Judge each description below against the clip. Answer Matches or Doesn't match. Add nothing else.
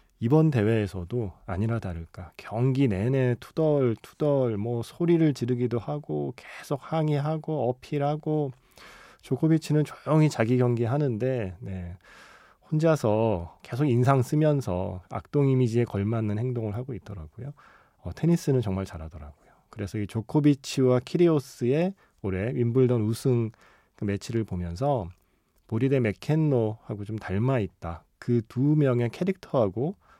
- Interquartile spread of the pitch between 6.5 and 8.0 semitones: Doesn't match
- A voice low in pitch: Matches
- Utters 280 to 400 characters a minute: Matches